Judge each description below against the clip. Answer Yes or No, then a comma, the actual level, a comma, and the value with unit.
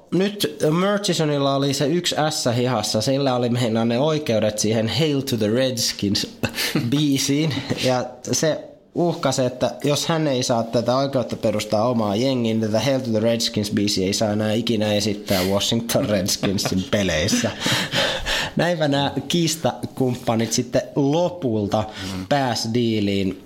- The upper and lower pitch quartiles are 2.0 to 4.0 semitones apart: No, average, 4.4 semitones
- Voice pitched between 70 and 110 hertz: No, low, 125 Hz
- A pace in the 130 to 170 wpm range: Yes, average, 135 wpm